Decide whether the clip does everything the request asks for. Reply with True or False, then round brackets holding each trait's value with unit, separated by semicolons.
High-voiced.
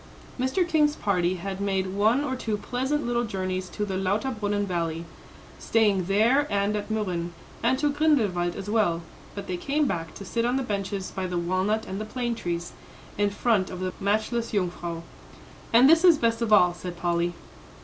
True (205 Hz)